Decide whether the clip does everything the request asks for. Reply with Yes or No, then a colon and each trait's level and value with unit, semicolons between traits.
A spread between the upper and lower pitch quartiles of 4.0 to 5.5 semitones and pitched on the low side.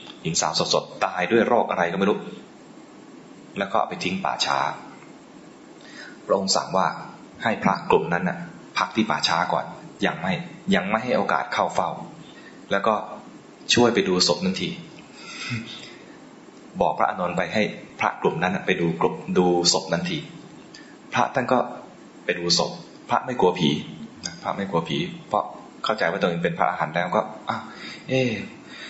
Yes: average, 5.1 semitones; very low, 95 Hz